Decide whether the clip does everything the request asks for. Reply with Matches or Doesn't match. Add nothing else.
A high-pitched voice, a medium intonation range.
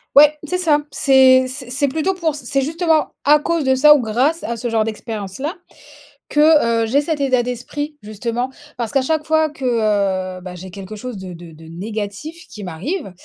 Doesn't match